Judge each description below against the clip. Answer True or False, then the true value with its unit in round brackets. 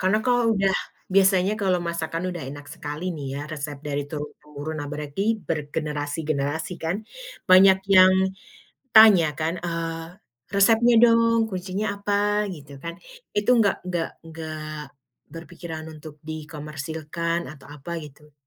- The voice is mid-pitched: True (165 Hz)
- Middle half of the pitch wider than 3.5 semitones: True (4.1 semitones)